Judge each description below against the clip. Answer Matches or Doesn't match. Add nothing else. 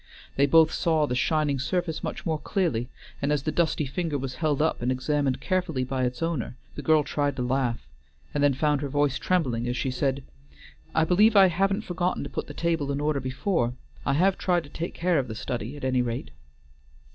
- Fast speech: Matches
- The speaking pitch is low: Doesn't match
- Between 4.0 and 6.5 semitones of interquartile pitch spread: Matches